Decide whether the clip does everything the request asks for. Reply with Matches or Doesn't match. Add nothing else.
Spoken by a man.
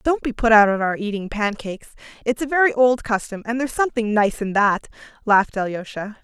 Doesn't match